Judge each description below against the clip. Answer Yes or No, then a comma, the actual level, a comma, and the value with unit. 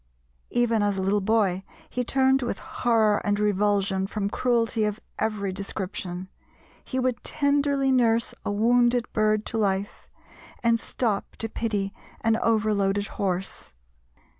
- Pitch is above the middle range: Yes, high, 215 Hz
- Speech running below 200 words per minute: Yes, slow, 135 wpm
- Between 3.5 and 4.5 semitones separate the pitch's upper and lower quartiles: No, average, 3.0 semitones